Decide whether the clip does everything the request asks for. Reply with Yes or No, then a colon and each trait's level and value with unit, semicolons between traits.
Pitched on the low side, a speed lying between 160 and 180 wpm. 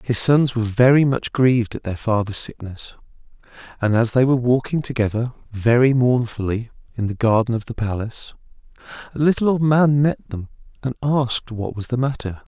Yes: low, 120 Hz; average, 170 wpm